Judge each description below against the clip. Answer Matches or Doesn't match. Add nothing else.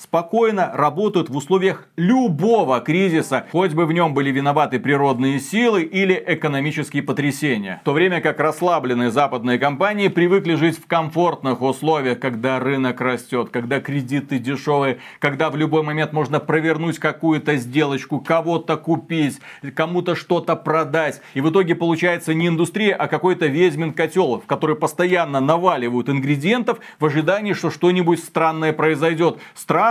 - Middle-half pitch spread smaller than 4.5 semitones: Matches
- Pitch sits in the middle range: Matches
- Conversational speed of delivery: Matches